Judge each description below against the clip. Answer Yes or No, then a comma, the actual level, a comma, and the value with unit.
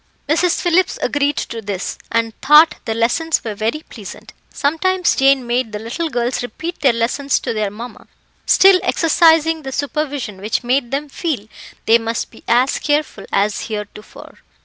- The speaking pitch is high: Yes, very high, 265 Hz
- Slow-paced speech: No, average, 160 wpm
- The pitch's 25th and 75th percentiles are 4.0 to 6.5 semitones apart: Yes, average, 5.3 semitones